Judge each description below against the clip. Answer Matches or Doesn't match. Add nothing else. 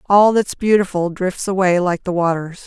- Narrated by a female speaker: Matches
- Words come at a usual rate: Matches